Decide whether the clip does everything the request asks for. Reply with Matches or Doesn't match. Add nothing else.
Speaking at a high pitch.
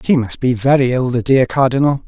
Doesn't match